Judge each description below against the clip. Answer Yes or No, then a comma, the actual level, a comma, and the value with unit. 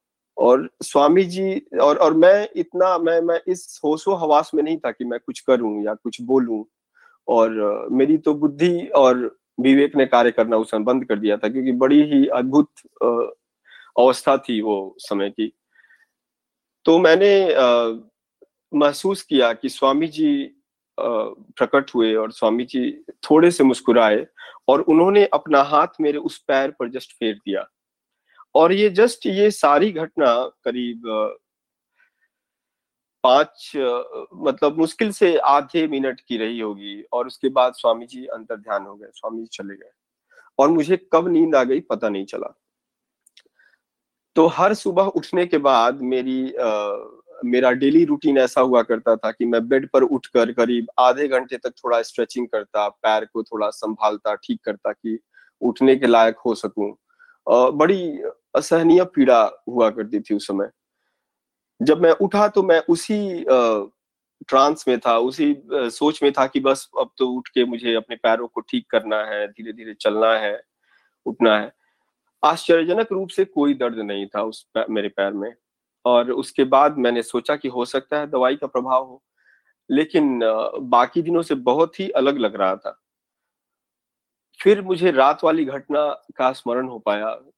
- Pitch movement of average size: No, wide, 7.6 semitones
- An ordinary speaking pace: Yes, average, 155 wpm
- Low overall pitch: Yes, low, 130 Hz